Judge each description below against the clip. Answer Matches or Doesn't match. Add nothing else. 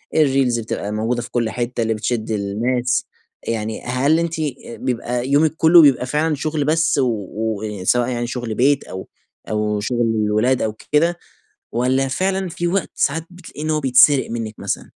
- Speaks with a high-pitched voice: Doesn't match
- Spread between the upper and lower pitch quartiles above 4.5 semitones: Matches